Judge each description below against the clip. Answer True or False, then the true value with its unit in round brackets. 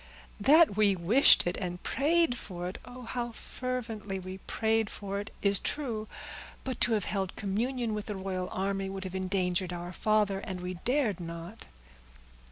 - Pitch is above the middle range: True (200 Hz)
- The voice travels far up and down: False (3.7 semitones)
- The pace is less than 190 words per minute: True (160 wpm)